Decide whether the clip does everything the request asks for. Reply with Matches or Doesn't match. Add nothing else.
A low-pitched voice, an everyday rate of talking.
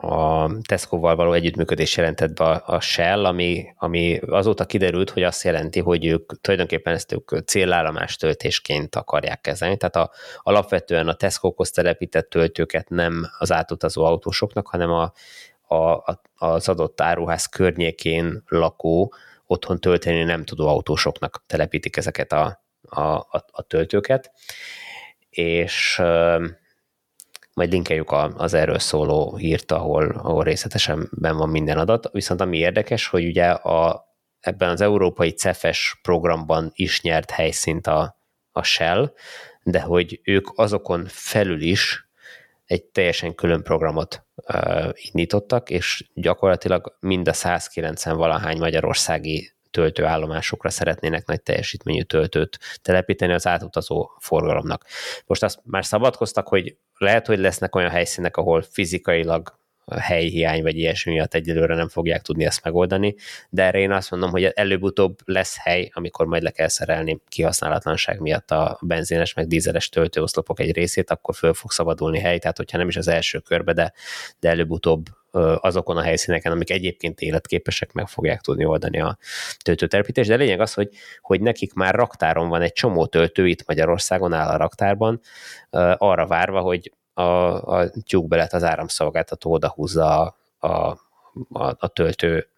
Matches